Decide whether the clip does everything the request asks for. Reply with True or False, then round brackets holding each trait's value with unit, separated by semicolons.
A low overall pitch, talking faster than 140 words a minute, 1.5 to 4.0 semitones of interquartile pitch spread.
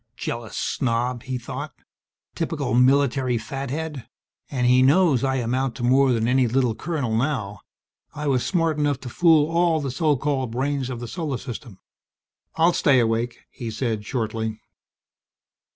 True (130 Hz; 150 wpm; 3.3 semitones)